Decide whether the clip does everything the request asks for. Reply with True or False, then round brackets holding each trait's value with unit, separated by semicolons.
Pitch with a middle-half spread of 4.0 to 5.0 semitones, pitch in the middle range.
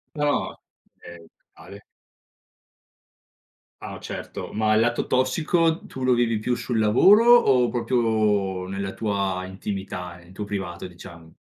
False (4.5 semitones; 105 Hz)